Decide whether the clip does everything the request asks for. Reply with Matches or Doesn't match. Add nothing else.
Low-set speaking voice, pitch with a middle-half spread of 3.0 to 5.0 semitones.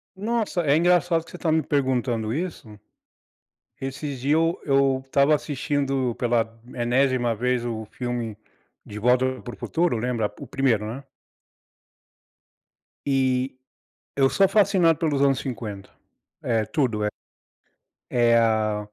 Matches